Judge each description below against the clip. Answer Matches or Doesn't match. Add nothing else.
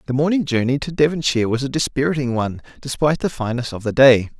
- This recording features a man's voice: Matches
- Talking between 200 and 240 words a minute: Matches